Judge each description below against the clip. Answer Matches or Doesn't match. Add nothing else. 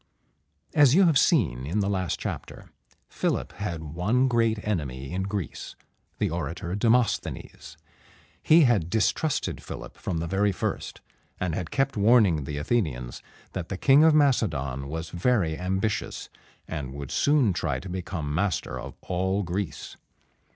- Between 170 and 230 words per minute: Doesn't match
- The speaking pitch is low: Matches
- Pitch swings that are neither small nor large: Doesn't match